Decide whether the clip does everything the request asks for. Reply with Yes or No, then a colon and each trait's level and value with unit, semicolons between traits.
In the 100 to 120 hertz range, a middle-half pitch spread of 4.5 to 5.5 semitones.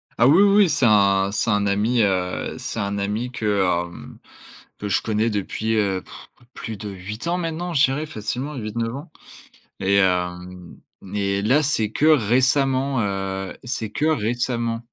Yes: low, 110 Hz; average, 4.9 semitones